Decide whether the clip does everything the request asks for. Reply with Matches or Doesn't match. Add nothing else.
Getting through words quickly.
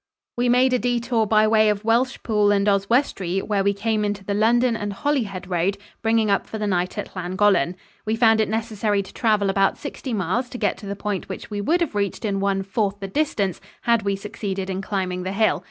Matches